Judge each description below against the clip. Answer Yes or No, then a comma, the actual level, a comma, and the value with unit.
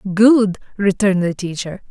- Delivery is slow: Yes, slow, 125 wpm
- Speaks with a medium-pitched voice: No, high, 195 Hz